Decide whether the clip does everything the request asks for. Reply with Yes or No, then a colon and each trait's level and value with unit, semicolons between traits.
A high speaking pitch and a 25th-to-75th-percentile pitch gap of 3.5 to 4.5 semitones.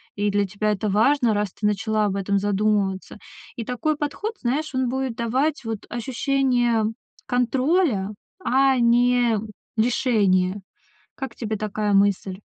Yes: high, 225 Hz; average, 3.9 semitones